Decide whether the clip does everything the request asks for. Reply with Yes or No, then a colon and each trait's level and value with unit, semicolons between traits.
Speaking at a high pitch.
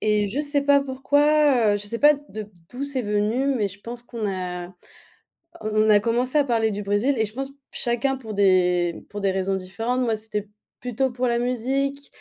Yes: high, 230 Hz